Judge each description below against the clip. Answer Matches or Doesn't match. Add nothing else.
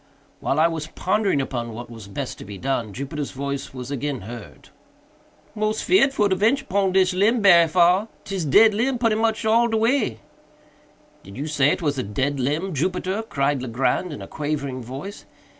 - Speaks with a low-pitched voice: Doesn't match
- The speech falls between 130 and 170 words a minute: Doesn't match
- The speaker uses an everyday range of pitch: Doesn't match